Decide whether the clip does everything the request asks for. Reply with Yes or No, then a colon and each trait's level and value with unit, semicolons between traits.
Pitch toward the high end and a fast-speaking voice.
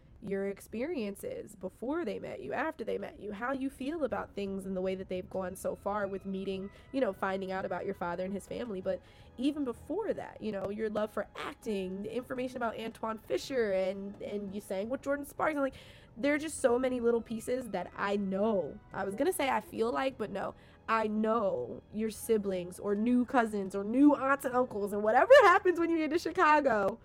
Yes: high, 220 Hz; fast, 215 wpm